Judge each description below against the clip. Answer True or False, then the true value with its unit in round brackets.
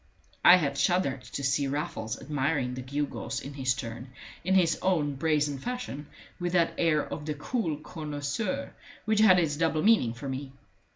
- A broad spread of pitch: False (4.2 semitones)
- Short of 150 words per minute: False (170 wpm)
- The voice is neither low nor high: True (150 Hz)